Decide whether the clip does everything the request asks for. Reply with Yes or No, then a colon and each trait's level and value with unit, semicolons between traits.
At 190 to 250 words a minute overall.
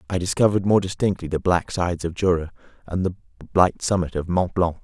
Yes: average, 200 wpm